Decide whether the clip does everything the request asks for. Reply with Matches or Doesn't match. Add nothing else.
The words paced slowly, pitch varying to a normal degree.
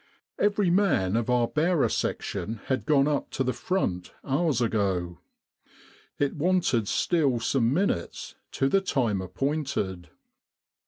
Doesn't match